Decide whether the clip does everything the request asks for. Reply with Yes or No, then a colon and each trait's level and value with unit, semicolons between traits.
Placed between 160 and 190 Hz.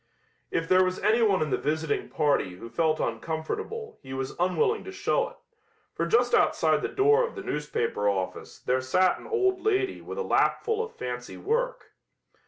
Yes: medium, 185 Hz